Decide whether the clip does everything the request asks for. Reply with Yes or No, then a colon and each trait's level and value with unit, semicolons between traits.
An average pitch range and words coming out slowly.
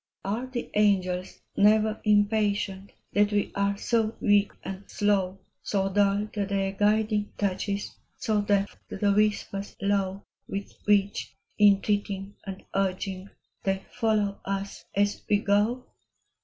No: narrow, 1.1 semitones; slow, 130 wpm